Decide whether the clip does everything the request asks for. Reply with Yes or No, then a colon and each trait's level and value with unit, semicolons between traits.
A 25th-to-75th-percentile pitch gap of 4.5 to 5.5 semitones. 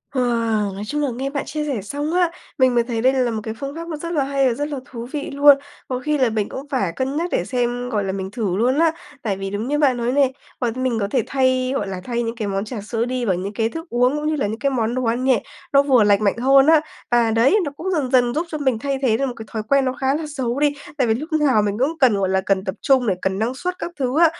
No: average, 4.0 semitones